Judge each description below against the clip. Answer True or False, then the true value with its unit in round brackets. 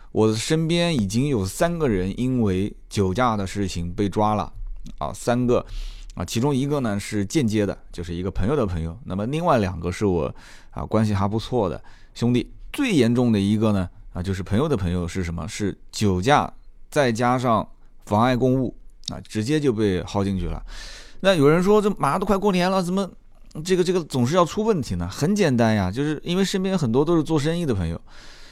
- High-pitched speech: False (115 Hz)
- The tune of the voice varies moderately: False (7.6 semitones)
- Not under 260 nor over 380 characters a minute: True (295 characters per minute)